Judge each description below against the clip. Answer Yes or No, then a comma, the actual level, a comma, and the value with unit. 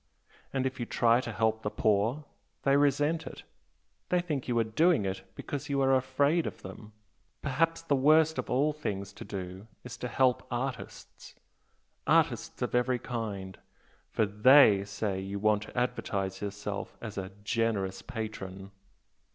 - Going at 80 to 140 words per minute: No, average, 160 wpm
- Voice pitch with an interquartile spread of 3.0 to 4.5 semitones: No, average, 5.2 semitones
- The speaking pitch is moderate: No, low, 115 Hz